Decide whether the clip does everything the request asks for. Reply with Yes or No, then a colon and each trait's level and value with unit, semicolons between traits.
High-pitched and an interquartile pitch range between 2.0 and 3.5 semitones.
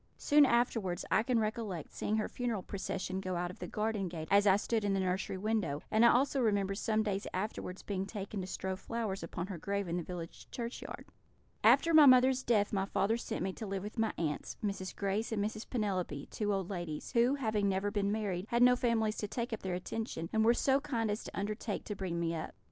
Yes: high, 205 Hz; average, 3.2 semitones